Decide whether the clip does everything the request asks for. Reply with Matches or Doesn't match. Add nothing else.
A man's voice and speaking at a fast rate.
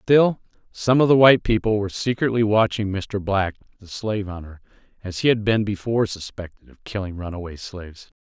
Doesn't match